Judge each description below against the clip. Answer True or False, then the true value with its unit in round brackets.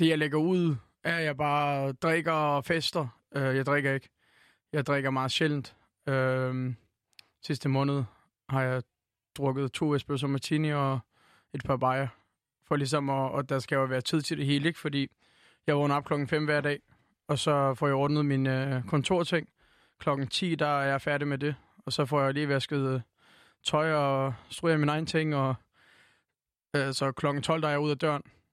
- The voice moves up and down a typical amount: False (2.0 semitones)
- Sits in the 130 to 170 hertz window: True (140 Hz)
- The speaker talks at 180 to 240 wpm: True (190 wpm)